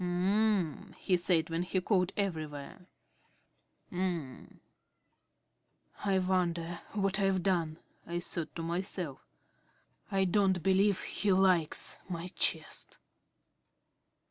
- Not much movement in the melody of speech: Yes, narrow, 2.2 semitones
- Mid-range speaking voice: Yes, medium, 180 Hz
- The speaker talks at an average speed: No, slow, 100 wpm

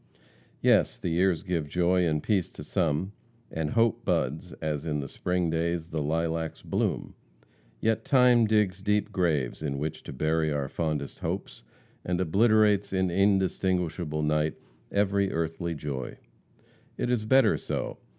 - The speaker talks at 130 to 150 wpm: Yes, average, 145 wpm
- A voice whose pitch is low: Yes, very low, 85 Hz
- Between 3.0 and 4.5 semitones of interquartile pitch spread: Yes, average, 4.1 semitones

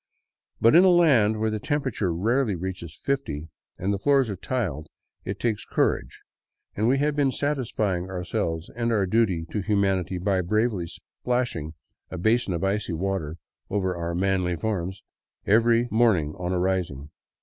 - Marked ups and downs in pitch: No, average, 4.8 semitones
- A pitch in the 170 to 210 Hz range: No, low, 100 Hz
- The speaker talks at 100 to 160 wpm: Yes, average, 155 wpm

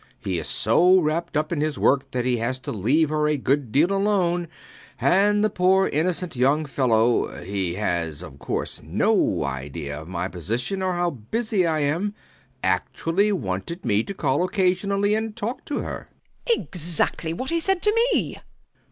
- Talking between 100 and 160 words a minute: No, average, 175 wpm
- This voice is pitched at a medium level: Yes, medium, 155 Hz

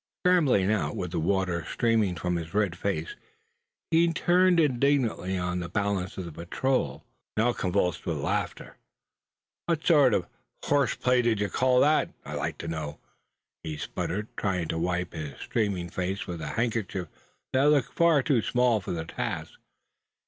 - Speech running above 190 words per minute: No, average, 160 wpm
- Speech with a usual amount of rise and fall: No, wide, 6.5 semitones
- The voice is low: Yes, low, 100 Hz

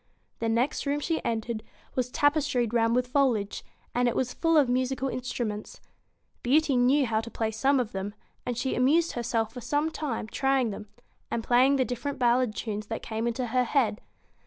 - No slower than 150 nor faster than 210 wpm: Yes, average, 185 wpm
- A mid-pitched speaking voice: No, high, 245 Hz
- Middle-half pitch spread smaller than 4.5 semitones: Yes, average, 3.0 semitones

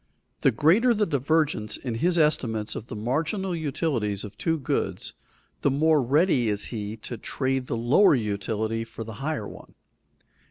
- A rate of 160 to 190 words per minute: Yes, average, 165 wpm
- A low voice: Yes, low, 130 Hz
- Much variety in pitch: Yes, wide, 6.2 semitones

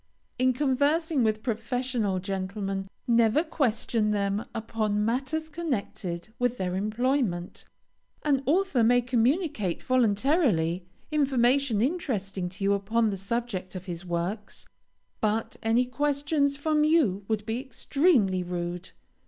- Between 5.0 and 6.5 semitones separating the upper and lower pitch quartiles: Yes, wide, 5.6 semitones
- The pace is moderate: No, slow, 120 wpm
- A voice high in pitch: Yes, high, 230 Hz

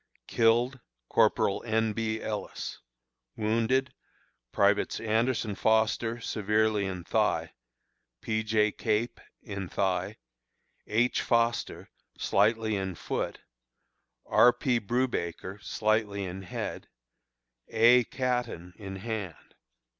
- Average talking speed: No, slow, 95 wpm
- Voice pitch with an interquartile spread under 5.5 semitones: Yes, narrow, 2.5 semitones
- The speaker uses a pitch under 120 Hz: Yes, low, 110 Hz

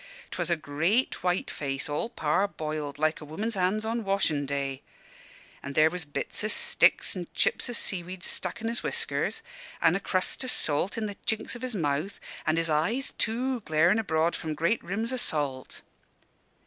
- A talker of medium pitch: Yes, medium, 180 Hz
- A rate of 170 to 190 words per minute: Yes, average, 185 wpm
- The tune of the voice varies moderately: No, wide, 6.1 semitones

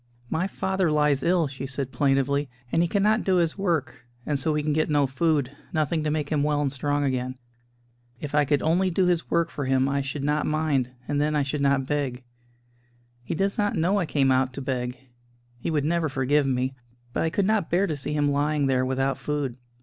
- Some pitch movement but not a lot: Yes, average, 3.0 semitones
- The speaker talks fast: Yes, fast, 220 wpm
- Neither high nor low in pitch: Yes, medium, 145 Hz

